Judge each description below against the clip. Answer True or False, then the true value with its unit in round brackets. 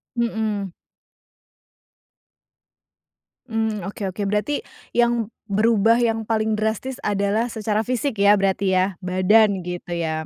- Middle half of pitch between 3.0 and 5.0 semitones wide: False (2.4 semitones)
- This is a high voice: True (215 Hz)